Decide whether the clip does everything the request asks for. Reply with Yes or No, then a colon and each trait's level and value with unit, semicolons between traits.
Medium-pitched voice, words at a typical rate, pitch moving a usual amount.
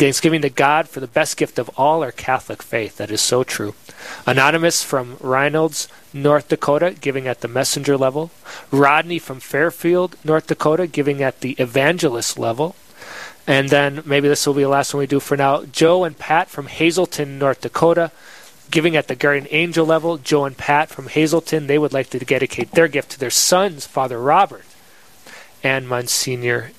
Yes: medium, 145 Hz; average, 180 wpm; average, 3.2 semitones